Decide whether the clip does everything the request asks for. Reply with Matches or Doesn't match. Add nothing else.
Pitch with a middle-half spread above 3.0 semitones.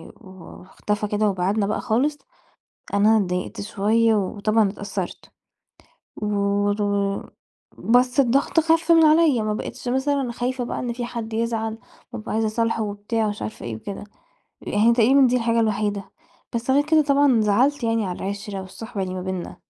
Matches